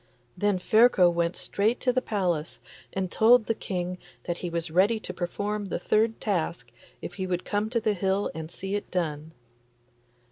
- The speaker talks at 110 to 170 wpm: No, average, 180 wpm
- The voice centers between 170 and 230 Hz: Yes, high, 190 Hz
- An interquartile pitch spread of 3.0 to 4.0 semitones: Yes, average, 3.5 semitones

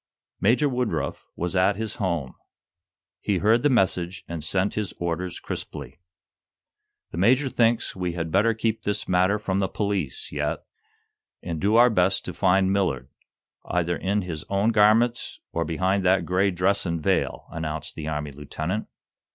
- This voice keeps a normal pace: Yes, average, 160 wpm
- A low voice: Yes, very low, 95 Hz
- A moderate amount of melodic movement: Yes, average, 3.7 semitones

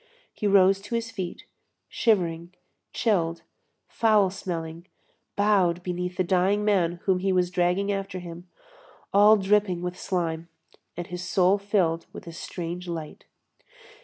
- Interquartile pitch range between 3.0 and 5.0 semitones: No, narrow, 2.4 semitones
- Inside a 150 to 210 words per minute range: No, slow, 135 wpm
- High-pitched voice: No, medium, 180 Hz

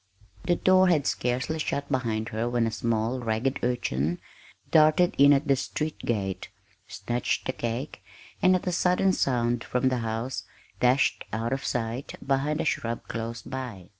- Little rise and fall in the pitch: No, average, 3.8 semitones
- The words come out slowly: No, average, 165 wpm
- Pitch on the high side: No, low, 125 Hz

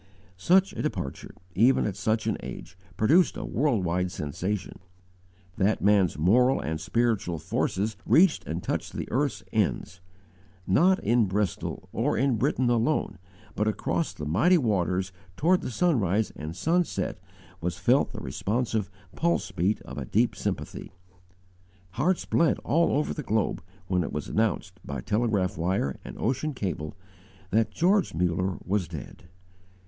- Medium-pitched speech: No, low, 105 Hz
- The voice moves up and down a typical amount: No, wide, 6.1 semitones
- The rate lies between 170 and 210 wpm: No, average, 145 wpm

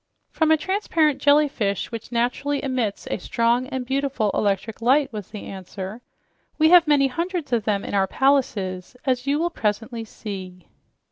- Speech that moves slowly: No, average, 160 wpm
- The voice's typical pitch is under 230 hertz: No, high, 245 Hz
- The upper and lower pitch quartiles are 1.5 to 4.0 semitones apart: No, wide, 5.5 semitones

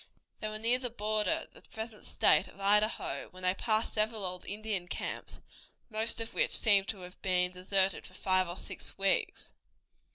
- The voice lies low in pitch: No, high, 205 Hz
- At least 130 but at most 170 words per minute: No, average, 185 wpm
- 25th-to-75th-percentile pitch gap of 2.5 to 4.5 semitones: Yes, average, 2.8 semitones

